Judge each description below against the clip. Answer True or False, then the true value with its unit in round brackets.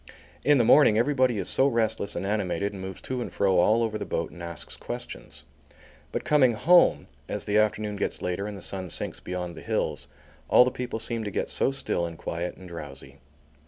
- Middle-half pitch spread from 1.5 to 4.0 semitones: False (4.6 semitones)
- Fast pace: True (210 wpm)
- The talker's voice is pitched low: True (105 Hz)